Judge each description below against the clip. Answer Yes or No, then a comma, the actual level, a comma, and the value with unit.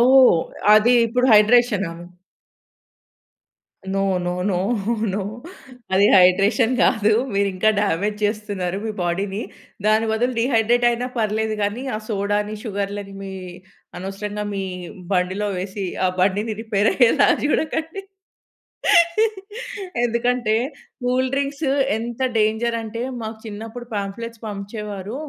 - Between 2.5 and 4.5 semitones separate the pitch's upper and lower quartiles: Yes, average, 2.9 semitones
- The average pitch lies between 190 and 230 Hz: Yes, high, 215 Hz